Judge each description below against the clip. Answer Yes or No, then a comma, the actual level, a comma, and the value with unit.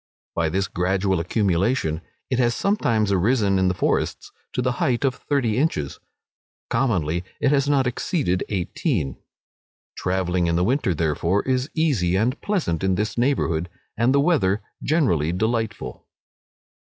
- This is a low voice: Yes, low, 105 Hz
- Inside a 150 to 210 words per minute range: No, average, 140 wpm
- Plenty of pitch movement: Yes, wide, 6.6 semitones